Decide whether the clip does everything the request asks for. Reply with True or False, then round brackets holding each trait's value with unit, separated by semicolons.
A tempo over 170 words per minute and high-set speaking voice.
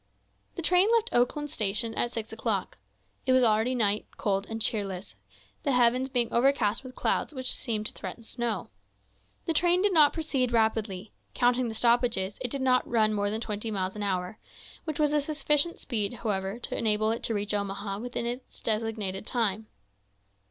True (180 wpm; 230 Hz)